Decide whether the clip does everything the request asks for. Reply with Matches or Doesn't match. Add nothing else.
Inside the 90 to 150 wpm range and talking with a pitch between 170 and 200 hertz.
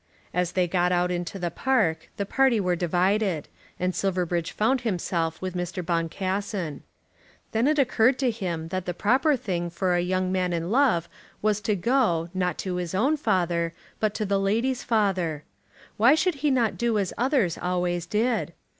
Doesn't match